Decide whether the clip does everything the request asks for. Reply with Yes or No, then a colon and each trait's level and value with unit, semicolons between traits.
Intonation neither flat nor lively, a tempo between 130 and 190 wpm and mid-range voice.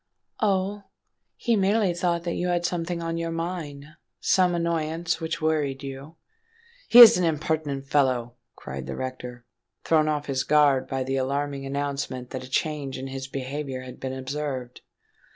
Yes: average, 3.9 semitones; average, 155 wpm; medium, 145 Hz